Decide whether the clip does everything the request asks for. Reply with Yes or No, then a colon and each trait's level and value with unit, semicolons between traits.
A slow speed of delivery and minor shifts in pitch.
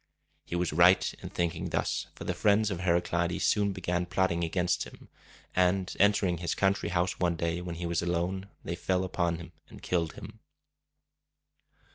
No: average, 170 wpm; narrow, 1.6 semitones